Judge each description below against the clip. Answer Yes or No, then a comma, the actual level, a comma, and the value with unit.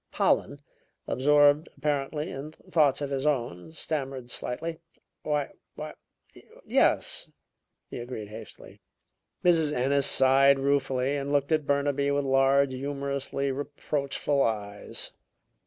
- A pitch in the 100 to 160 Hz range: Yes, medium, 140 Hz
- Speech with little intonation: Yes, narrow, 1.5 semitones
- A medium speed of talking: No, slow, 110 wpm